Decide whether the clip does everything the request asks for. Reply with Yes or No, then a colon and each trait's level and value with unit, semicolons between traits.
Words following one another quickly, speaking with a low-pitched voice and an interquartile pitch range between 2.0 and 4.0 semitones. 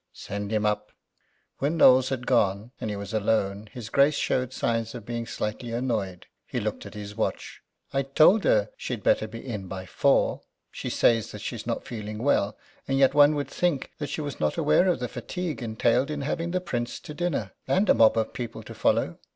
No: fast, 210 wpm; low, 120 Hz; average, 5.1 semitones